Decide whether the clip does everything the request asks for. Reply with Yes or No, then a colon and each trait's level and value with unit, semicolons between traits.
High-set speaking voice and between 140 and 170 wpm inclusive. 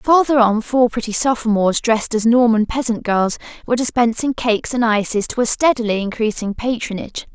Yes: high, 230 Hz; average, 165 wpm